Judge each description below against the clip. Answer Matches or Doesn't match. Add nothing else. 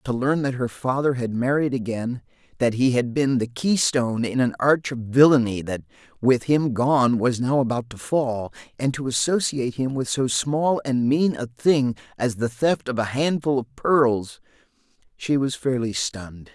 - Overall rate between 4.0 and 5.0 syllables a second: Matches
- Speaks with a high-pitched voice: Doesn't match